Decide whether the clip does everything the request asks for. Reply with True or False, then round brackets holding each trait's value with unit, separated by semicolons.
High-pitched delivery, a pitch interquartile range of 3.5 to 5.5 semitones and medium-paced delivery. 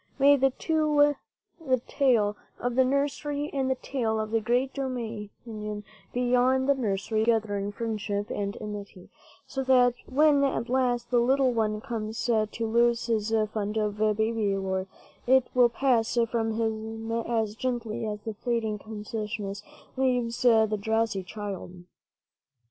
False (230 Hz; 3.1 semitones; 145 wpm)